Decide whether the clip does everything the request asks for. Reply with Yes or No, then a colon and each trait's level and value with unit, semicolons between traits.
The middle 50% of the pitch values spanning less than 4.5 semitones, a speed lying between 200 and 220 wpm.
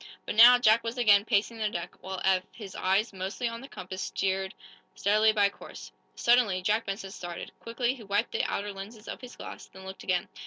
Yes: average, 3.3 semitones; fast, 205 wpm